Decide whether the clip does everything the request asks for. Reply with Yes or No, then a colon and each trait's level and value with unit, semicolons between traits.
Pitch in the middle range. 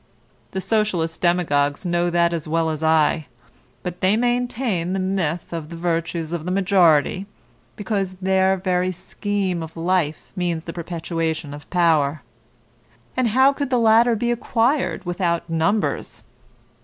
Yes: medium, 175 Hz